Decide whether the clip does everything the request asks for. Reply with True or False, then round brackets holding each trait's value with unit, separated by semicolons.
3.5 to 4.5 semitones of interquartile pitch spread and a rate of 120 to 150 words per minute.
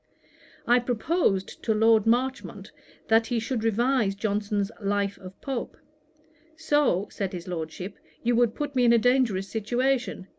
True (3.8 semitones; 145 wpm)